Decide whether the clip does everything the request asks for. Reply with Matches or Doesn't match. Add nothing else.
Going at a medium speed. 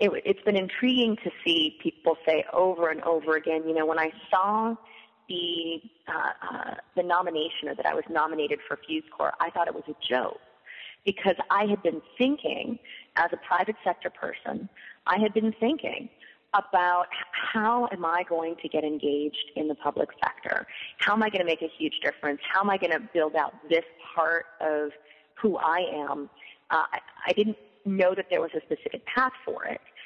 Matches